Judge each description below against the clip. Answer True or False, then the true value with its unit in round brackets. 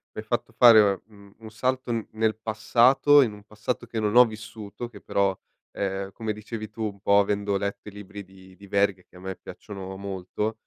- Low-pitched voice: True (105 Hz)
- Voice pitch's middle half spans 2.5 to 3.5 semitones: False (2.0 semitones)